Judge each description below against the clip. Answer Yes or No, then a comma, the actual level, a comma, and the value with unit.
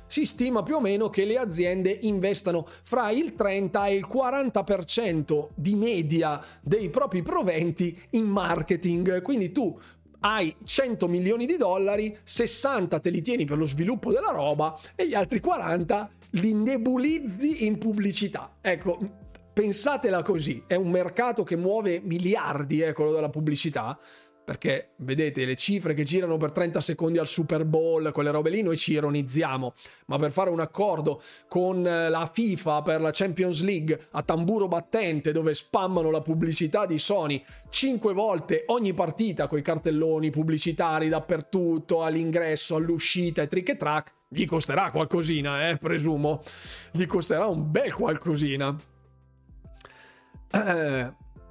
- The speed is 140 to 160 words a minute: Yes, average, 145 wpm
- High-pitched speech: No, medium, 175 Hz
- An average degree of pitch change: Yes, average, 4.4 semitones